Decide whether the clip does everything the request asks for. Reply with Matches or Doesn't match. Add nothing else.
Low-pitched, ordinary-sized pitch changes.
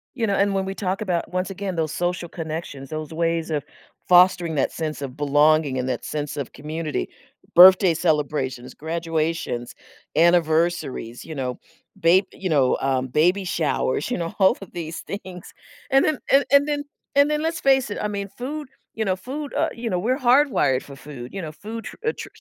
Doesn't match